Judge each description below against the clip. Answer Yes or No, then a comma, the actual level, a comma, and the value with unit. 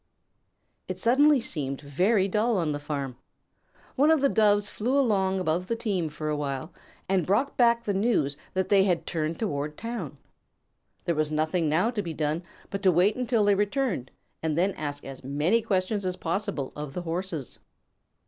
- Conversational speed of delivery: Yes, average, 180 wpm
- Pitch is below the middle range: No, medium, 185 Hz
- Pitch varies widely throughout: Yes, wide, 5.9 semitones